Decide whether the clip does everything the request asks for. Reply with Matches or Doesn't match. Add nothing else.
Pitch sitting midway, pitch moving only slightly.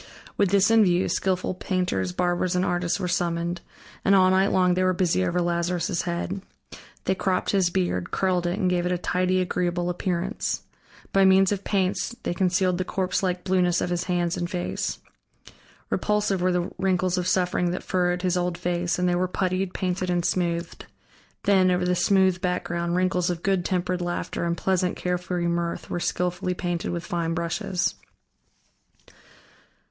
Matches